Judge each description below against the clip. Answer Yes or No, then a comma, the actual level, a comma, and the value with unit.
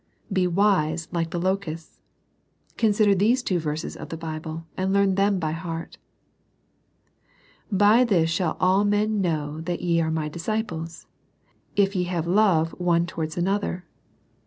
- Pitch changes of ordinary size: Yes, average, 3.4 semitones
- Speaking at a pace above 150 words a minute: No, average, 145 wpm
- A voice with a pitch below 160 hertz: No, medium, 175 Hz